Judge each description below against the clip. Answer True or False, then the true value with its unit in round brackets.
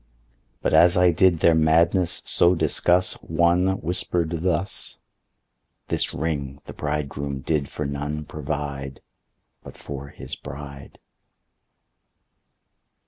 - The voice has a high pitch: False (80 Hz)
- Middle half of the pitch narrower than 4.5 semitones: True (3.6 semitones)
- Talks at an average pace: False (105 wpm)